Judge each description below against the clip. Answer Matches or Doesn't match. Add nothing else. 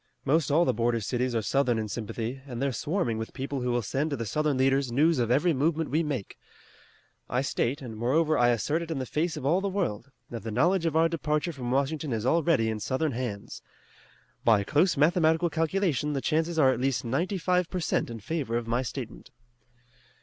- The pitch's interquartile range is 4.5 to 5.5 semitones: Matches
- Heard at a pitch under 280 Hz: Matches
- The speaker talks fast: Matches